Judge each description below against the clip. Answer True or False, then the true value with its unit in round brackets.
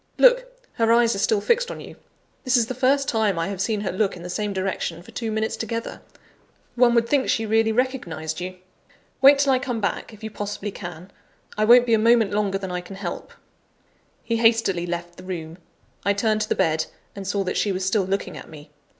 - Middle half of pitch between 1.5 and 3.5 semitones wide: False (4.0 semitones)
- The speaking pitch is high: True (210 Hz)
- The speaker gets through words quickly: True (225 wpm)